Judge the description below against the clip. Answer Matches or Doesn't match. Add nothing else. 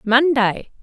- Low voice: Doesn't match